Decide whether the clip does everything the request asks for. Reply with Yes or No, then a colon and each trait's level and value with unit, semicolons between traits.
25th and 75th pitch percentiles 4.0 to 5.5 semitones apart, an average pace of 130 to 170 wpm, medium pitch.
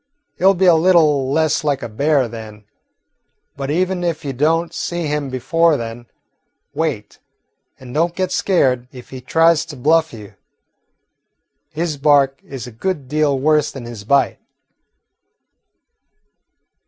Yes: average, 4.3 semitones; average, 140 wpm; medium, 145 Hz